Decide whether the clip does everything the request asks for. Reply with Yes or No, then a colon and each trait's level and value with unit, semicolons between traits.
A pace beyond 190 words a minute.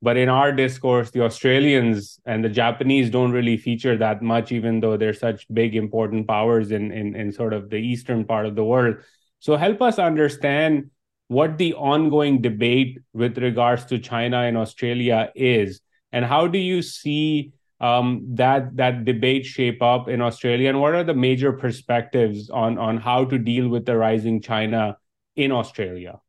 No: average, 175 wpm